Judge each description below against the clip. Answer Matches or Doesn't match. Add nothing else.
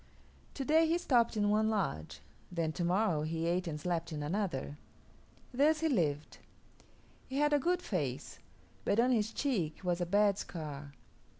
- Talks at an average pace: Matches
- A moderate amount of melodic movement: Doesn't match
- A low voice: Doesn't match